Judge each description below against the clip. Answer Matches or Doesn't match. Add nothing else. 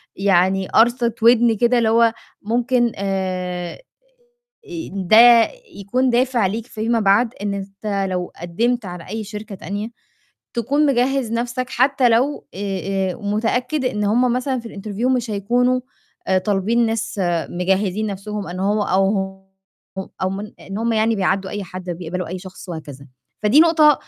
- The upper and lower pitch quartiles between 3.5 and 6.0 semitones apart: Matches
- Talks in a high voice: Matches